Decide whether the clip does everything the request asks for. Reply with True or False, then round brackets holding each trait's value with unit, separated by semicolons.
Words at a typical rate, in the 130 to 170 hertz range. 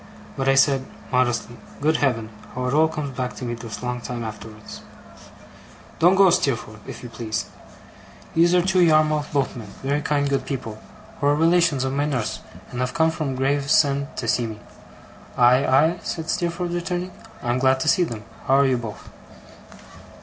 True (180 wpm; 135 Hz)